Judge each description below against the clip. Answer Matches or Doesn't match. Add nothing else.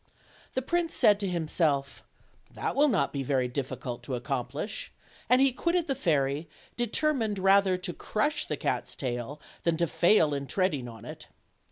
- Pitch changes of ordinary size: Doesn't match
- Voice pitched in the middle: Matches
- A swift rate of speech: Doesn't match